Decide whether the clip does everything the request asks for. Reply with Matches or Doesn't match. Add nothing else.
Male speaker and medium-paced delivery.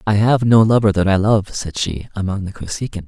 Doesn't match